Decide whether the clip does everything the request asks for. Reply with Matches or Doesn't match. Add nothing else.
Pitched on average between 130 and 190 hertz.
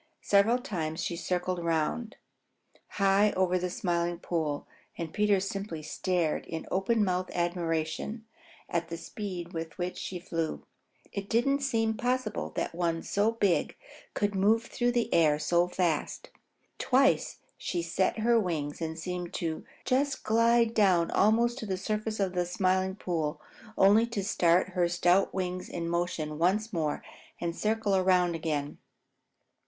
Matches